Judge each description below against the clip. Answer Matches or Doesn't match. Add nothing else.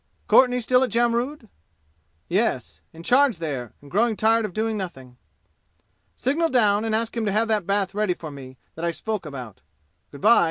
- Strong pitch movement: Matches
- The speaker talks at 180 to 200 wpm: Matches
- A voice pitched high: Matches